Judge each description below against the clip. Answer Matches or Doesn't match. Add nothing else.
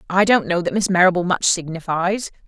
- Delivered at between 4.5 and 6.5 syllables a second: Matches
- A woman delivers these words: Matches